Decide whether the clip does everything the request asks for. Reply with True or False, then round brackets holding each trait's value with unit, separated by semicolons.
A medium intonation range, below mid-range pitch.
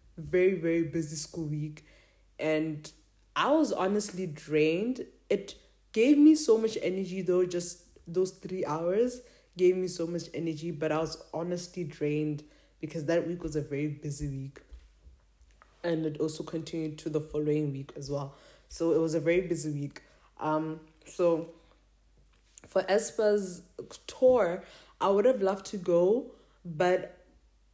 False (3.4 semitones; 165 Hz)